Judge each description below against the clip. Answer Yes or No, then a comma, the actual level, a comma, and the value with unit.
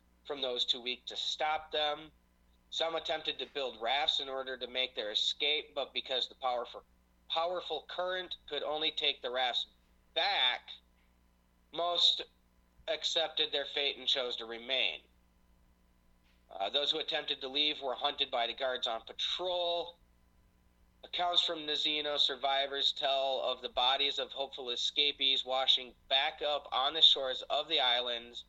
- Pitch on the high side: No, low, 135 Hz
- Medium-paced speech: Yes, average, 150 wpm